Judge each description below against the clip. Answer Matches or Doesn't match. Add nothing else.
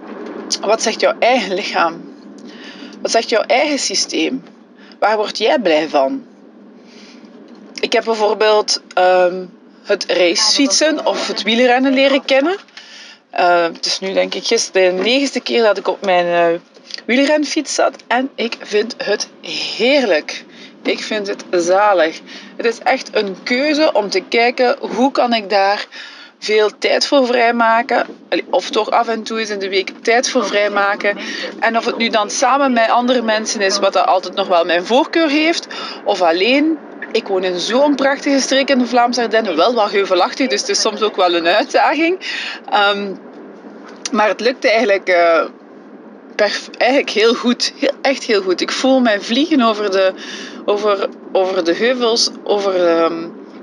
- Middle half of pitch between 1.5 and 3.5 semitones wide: Doesn't match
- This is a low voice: Doesn't match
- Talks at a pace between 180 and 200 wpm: Doesn't match